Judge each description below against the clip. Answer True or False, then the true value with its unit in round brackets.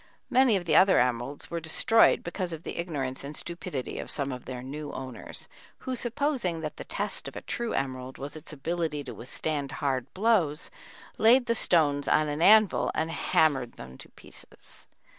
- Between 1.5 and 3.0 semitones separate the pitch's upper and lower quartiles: False (5.3 semitones)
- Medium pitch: True (155 Hz)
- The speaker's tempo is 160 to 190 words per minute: True (180 wpm)